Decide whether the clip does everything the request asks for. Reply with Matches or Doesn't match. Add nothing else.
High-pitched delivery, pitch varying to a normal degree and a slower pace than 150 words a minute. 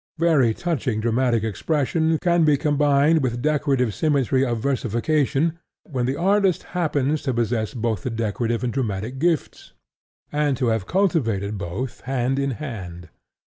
Doesn't match